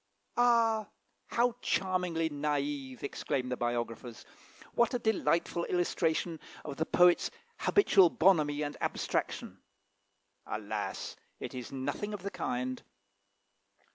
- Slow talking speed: Yes, slow, 110 wpm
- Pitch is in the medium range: Yes, medium, 160 Hz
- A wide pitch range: Yes, wide, 6.0 semitones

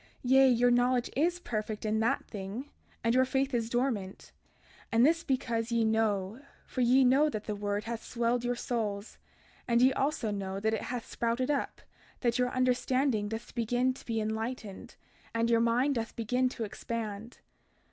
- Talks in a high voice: Yes, high, 235 Hz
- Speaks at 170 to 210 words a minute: Yes, average, 175 wpm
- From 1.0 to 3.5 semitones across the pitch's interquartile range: Yes, narrow, 2.6 semitones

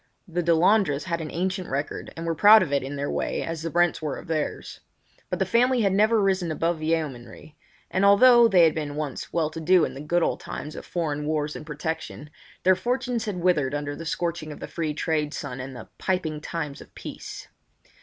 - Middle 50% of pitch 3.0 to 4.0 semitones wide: Yes, average, 3.7 semitones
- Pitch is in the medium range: Yes, medium, 165 Hz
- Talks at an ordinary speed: No, fast, 215 wpm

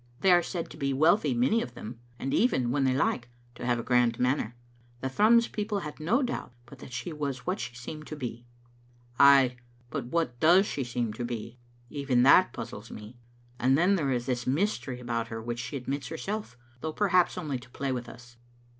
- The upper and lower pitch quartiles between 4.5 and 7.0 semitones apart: Yes, average, 5.1 semitones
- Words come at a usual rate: No, fast, 215 wpm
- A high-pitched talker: No, low, 130 Hz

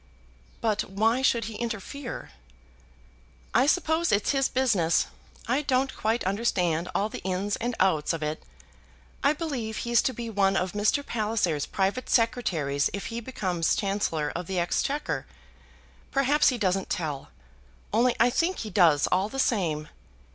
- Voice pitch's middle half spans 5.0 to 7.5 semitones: Yes, wide, 5.4 semitones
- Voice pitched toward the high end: Yes, high, 215 Hz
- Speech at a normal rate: Yes, average, 150 wpm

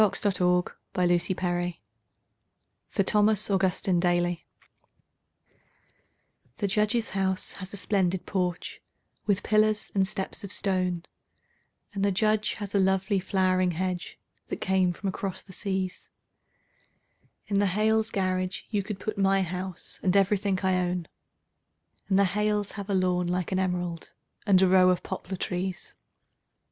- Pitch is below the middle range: No, high, 190 Hz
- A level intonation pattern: Yes, narrow, 1.7 semitones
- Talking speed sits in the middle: Yes, average, 145 wpm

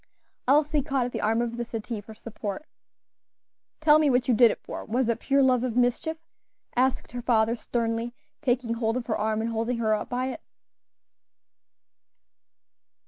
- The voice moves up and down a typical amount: No, narrow, 2.2 semitones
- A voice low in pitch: No, high, 240 Hz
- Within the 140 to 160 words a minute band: No, average, 175 wpm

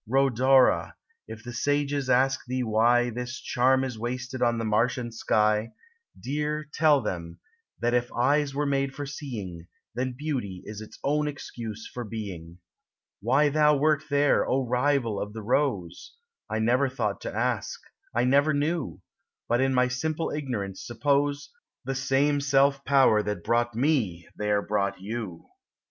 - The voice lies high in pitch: No, low, 125 Hz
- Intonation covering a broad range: No, average, 4.2 semitones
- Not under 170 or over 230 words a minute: No, average, 155 wpm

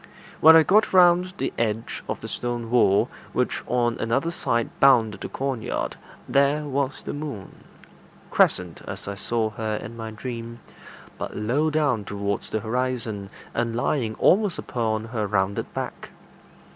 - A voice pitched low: Yes, low, 115 Hz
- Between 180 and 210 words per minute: No, average, 155 wpm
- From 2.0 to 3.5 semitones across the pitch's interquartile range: No, average, 4.2 semitones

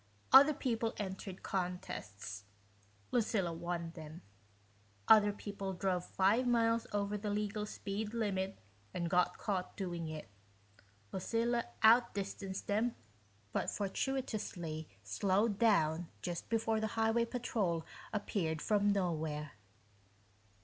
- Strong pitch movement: No, average, 4.1 semitones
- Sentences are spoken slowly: Yes, slow, 110 wpm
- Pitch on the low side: No, high, 200 Hz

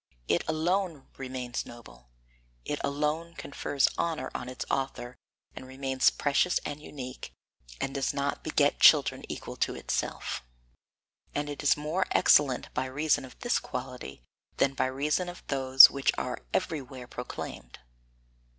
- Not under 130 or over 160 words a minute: Yes, average, 140 wpm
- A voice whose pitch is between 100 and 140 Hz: Yes, low, 135 Hz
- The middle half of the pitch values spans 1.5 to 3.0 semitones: Yes, average, 2.7 semitones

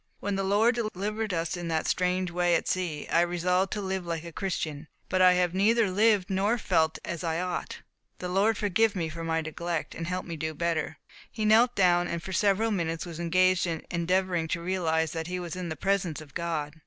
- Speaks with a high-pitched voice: No, medium, 180 Hz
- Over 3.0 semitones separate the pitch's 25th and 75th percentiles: No, narrow, 2.6 semitones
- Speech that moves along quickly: Yes, fast, 220 wpm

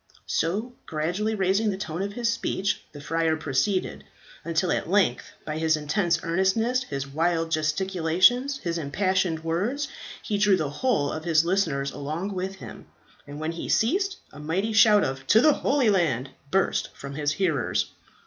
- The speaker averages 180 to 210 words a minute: No, average, 165 wpm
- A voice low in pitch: No, medium, 175 Hz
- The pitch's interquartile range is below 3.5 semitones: No, average, 4.8 semitones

